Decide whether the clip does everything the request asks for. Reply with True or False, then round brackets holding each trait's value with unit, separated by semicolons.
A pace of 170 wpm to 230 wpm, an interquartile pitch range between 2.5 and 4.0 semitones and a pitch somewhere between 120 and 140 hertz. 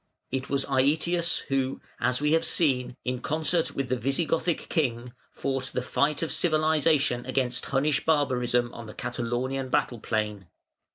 False (150 wpm; 3.7 semitones; 135 Hz)